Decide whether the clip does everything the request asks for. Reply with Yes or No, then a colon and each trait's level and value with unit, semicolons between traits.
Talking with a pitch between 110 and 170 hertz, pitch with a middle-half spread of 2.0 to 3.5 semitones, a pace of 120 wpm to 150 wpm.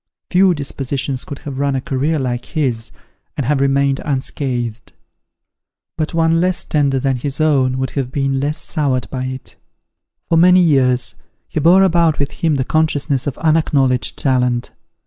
No: medium, 140 Hz; average, 3.2 semitones; average, 160 wpm